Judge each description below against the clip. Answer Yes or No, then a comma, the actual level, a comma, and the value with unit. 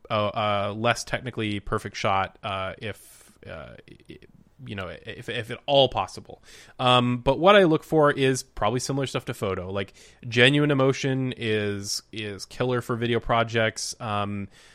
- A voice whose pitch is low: Yes, low, 120 Hz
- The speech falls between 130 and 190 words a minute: Yes, average, 160 wpm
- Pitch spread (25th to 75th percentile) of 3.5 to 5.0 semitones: Yes, average, 4.1 semitones